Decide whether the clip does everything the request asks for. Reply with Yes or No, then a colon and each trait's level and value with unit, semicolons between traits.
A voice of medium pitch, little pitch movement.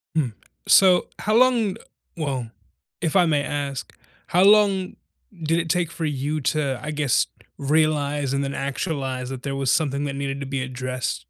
No: medium, 145 Hz; average, 3.2 semitones